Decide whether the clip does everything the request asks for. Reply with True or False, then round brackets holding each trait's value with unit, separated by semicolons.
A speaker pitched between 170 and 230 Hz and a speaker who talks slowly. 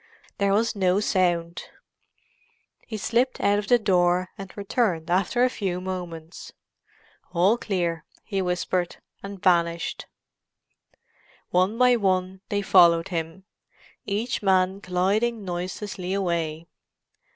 True (185 Hz; 115 wpm)